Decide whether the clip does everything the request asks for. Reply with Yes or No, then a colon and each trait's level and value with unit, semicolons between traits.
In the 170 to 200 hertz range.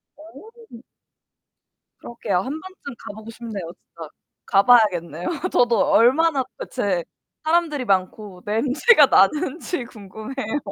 No: high, 235 Hz